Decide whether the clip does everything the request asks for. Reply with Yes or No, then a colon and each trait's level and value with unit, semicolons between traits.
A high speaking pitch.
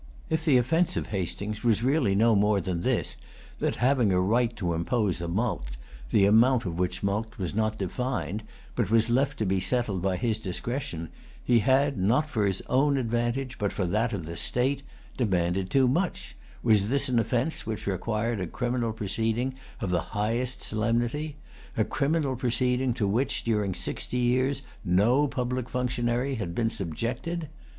No: low, 115 Hz